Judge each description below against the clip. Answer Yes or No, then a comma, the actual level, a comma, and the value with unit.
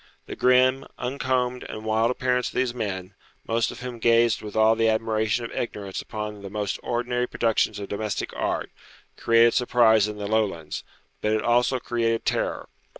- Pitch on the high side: No, low, 115 Hz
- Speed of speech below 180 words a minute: Yes, average, 170 wpm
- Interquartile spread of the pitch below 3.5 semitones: Yes, narrow, 2.4 semitones